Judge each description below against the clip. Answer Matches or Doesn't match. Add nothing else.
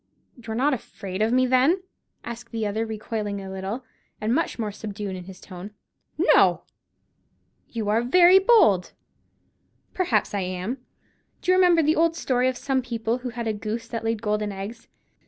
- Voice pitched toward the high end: Matches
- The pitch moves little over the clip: Doesn't match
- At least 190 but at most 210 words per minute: Doesn't match